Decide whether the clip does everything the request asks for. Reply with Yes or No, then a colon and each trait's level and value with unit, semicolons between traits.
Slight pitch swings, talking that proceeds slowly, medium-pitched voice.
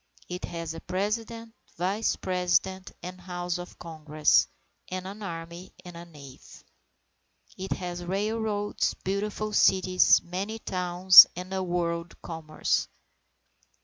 Yes: narrow, 2.3 semitones; slow, 115 wpm; medium, 180 Hz